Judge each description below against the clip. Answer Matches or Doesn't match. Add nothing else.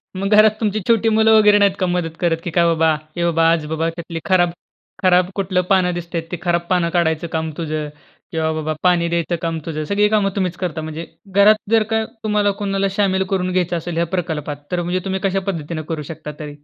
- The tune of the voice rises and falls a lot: Doesn't match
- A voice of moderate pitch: Matches